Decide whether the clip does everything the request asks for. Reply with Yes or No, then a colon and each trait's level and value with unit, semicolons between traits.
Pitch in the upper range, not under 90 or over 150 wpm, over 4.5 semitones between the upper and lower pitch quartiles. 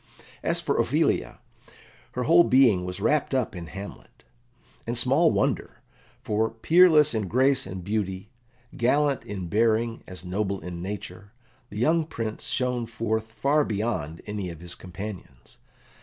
No: low, 110 Hz; average, 140 wpm; average, 5.2 semitones